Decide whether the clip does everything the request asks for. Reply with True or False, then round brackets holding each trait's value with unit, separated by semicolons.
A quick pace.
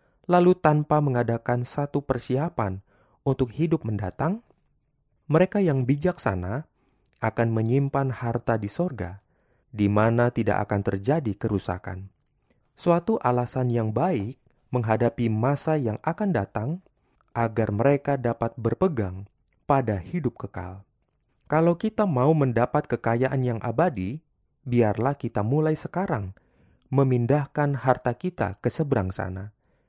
False (110 wpm)